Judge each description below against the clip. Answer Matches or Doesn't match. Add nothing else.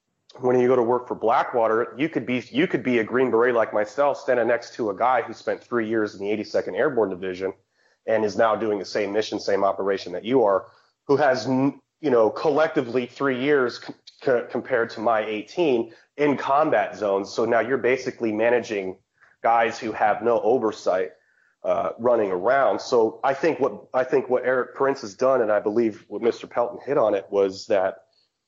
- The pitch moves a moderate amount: Matches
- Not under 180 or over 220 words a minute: Matches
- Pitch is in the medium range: Doesn't match